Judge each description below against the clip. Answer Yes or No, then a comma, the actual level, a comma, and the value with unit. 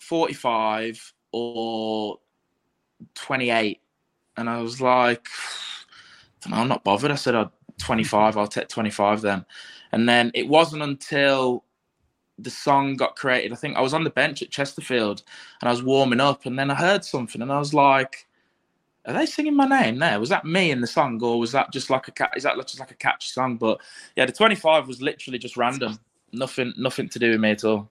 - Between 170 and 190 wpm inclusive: No, fast, 205 wpm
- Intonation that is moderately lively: Yes, average, 3.7 semitones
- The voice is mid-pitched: No, low, 125 Hz